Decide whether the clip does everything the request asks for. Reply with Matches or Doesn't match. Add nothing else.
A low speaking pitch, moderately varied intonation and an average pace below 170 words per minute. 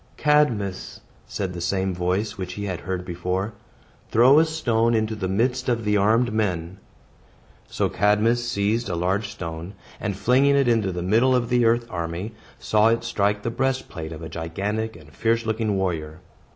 Doesn't match